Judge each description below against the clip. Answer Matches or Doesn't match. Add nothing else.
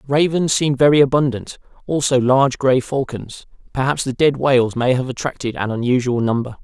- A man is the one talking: Matches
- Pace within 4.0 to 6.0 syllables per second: Matches